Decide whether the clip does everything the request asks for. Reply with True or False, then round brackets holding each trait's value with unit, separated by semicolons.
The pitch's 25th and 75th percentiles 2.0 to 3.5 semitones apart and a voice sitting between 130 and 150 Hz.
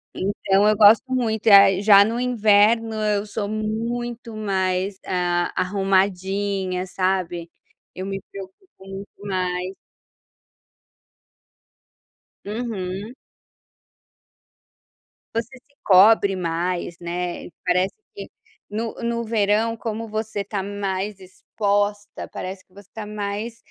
False (2.6 semitones; 200 Hz)